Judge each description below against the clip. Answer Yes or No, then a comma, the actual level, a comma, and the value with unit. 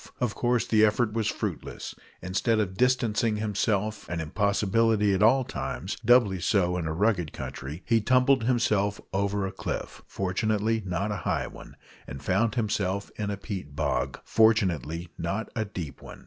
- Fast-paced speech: No, average, 160 wpm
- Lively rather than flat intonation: No, average, 3.3 semitones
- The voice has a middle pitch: No, low, 105 Hz